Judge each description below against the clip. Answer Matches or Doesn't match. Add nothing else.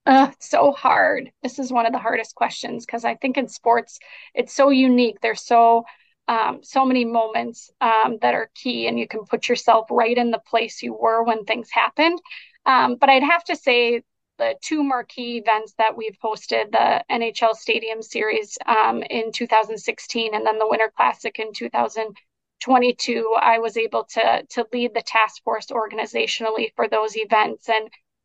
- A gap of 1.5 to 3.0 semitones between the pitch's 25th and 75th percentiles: Matches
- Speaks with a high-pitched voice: Matches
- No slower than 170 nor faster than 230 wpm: Matches